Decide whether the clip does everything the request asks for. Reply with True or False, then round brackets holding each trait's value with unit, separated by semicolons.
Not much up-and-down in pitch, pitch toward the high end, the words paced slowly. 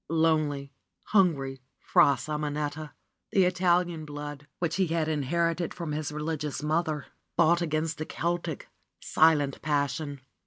False (2.3 semitones; 155 Hz; 125 wpm)